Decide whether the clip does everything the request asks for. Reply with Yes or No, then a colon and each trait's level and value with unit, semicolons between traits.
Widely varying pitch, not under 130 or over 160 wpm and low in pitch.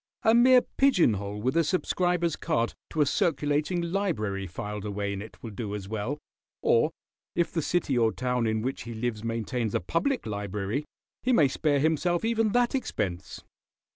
No: wide, 8.5 semitones; average, 175 wpm; low, 130 Hz